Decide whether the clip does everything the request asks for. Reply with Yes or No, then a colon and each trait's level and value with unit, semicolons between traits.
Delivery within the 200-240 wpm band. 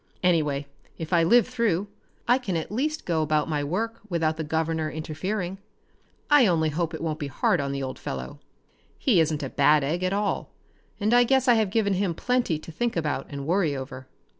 Yes: fast, 205 wpm